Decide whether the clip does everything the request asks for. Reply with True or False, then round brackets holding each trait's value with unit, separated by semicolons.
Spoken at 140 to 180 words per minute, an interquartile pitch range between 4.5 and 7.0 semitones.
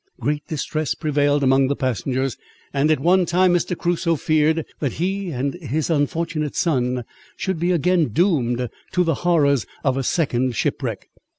False (160 wpm; 4.1 semitones)